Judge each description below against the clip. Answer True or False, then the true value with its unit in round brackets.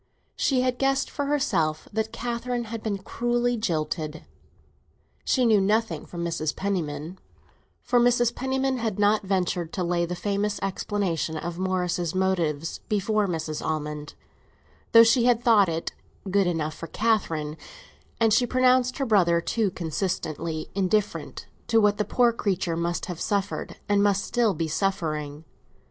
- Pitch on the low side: False (195 Hz)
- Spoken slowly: False (145 wpm)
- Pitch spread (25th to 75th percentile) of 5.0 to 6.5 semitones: True (5.5 semitones)